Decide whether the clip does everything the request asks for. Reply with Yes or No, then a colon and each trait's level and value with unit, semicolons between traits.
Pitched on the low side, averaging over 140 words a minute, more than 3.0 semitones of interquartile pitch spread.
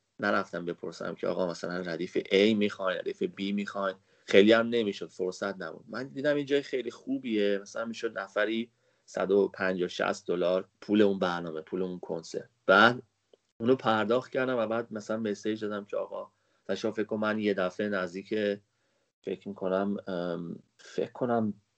No: low, 105 Hz; fast, 155 wpm; average, 2.7 semitones